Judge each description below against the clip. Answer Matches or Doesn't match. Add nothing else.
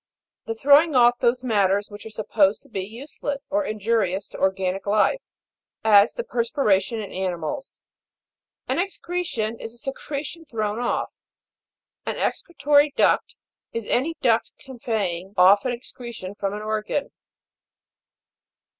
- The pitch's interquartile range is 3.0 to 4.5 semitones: Doesn't match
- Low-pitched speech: Doesn't match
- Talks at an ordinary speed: Doesn't match